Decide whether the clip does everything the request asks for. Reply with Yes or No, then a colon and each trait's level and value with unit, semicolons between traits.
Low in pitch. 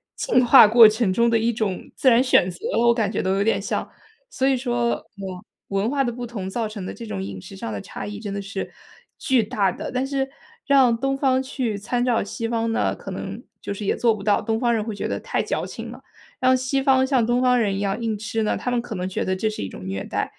No: high, 225 Hz